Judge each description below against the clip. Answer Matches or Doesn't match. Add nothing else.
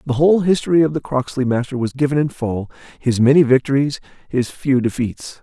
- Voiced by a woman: Doesn't match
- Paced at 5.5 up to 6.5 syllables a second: Matches